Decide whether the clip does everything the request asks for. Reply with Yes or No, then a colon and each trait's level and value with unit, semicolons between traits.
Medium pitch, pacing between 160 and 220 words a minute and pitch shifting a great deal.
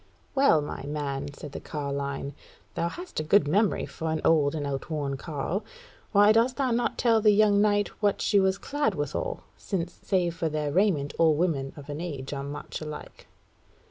Yes: medium, 165 Hz; average, 185 wpm; wide, 6.0 semitones